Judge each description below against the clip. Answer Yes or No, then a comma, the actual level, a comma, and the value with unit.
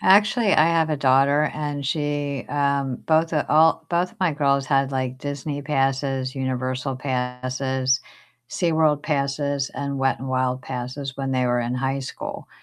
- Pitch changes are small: Yes, narrow, 2.3 semitones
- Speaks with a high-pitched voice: No, medium, 140 Hz